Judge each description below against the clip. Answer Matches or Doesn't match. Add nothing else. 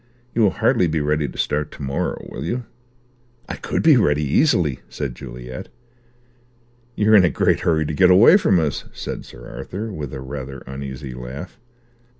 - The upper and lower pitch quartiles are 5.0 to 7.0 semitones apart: Matches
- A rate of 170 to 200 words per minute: Matches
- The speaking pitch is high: Doesn't match